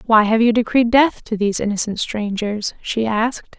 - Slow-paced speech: No, average, 185 wpm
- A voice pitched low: No, high, 220 Hz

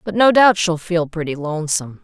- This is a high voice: No, medium, 175 Hz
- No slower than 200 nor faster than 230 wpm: Yes, fast, 205 wpm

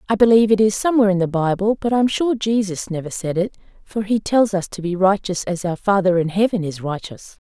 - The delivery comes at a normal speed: No, fast, 240 wpm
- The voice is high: Yes, high, 200 Hz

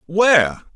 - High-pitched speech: No, medium, 170 Hz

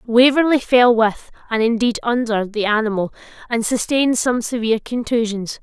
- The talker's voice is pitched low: No, high, 230 Hz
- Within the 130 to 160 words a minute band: Yes, average, 140 wpm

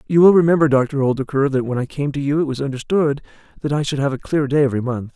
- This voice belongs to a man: Yes, male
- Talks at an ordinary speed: No, fast, 270 wpm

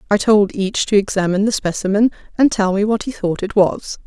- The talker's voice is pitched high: Yes, high, 205 Hz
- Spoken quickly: Yes, fast, 220 wpm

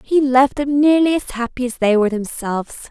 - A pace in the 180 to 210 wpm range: Yes, fast, 205 wpm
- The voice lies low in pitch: No, very high, 255 Hz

